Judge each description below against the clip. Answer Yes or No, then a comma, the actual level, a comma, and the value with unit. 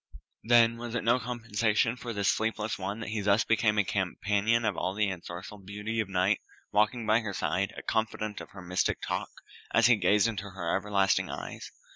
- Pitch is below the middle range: Yes, low, 105 Hz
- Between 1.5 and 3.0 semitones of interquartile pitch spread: Yes, narrow, 2.4 semitones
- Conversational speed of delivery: Yes, average, 195 wpm